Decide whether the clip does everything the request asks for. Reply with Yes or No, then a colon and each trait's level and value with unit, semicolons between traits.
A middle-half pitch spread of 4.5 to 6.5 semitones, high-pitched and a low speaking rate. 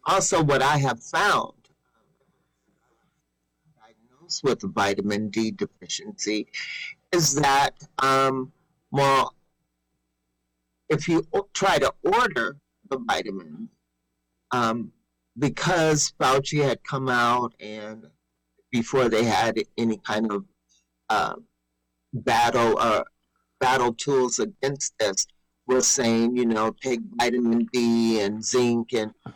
No: average, 5.1 semitones; low, 115 Hz; slow, 105 wpm